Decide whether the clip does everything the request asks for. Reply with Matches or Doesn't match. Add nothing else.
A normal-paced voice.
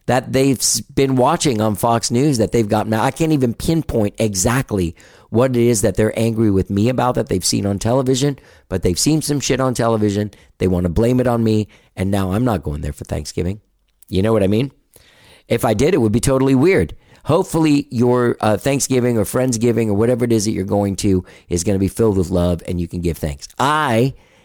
Doesn't match